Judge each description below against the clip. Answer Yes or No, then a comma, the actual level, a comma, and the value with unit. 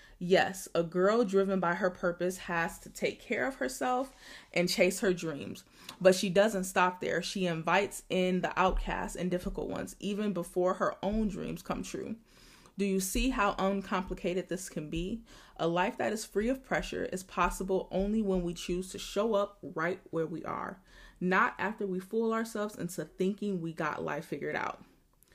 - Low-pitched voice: No, medium, 185 Hz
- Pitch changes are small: Yes, narrow, 2.3 semitones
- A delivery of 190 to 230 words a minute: No, average, 180 wpm